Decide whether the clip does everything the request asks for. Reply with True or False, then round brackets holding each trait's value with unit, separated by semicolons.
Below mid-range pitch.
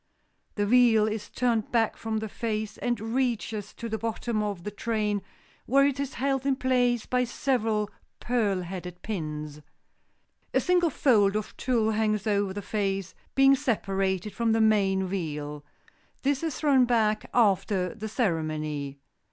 False (215 Hz)